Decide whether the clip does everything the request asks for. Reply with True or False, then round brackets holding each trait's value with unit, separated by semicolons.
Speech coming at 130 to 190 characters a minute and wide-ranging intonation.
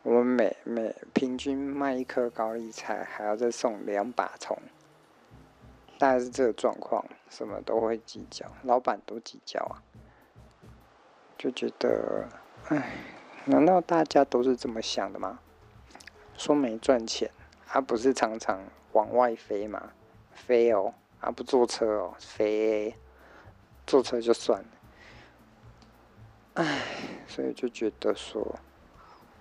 False (180 characters per minute; 2.9 semitones)